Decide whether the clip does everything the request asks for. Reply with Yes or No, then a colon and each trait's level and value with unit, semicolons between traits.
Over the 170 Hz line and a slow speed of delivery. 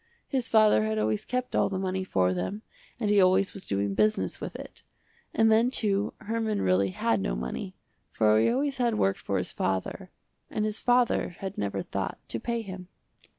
No: high, 190 Hz; average, 195 wpm